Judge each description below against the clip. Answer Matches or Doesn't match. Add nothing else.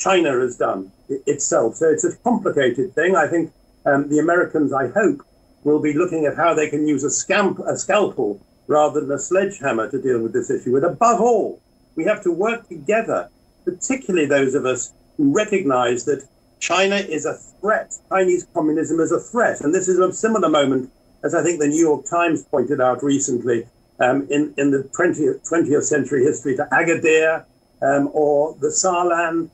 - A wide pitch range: Matches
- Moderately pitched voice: Matches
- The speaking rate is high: Doesn't match